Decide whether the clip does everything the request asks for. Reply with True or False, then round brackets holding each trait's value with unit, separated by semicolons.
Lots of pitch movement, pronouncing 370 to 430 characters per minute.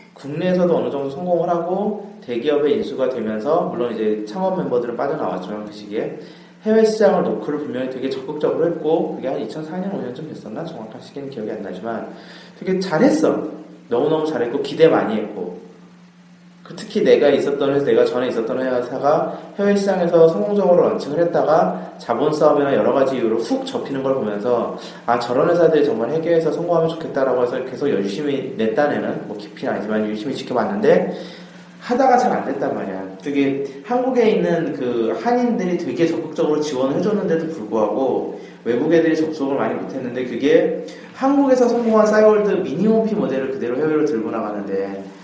True (6.1 semitones; 395 characters per minute)